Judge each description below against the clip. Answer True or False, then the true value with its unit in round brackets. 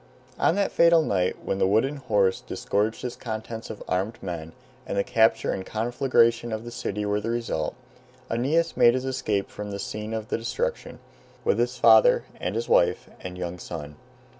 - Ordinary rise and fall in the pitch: True (4.4 semitones)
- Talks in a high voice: False (110 Hz)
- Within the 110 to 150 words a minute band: False (180 wpm)